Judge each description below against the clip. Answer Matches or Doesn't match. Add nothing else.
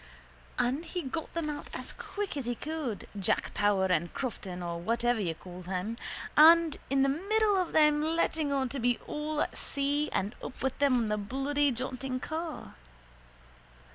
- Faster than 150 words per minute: Matches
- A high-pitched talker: Matches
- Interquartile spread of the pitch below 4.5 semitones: Doesn't match